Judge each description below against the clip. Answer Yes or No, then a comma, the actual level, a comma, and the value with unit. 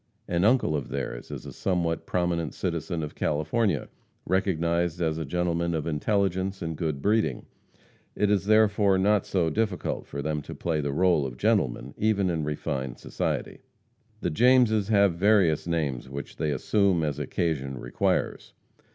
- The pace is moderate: Yes, average, 155 wpm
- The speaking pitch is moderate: No, very low, 85 Hz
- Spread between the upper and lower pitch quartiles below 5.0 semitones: Yes, average, 4.6 semitones